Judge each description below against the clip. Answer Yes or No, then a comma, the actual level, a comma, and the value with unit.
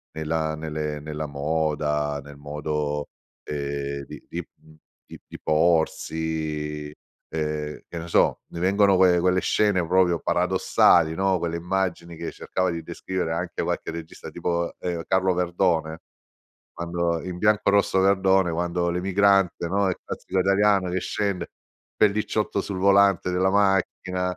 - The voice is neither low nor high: No, very low, 85 Hz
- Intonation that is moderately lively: Yes, average, 3.2 semitones